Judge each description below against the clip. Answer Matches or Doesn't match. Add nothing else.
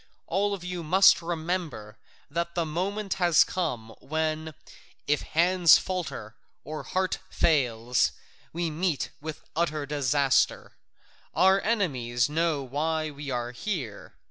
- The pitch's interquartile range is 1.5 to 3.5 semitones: Doesn't match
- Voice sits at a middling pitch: Matches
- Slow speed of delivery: Matches